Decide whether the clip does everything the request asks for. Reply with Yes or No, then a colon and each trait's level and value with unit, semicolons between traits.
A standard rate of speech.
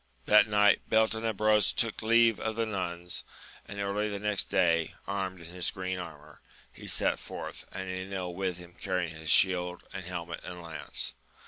Yes: average, 165 wpm